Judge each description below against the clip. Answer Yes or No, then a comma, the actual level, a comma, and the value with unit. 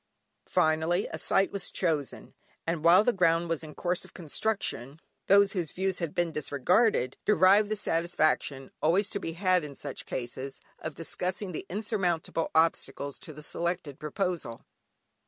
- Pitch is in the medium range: Yes, medium, 170 Hz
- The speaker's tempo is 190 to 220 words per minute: No, average, 155 wpm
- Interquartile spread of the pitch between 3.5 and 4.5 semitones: Yes, average, 3.8 semitones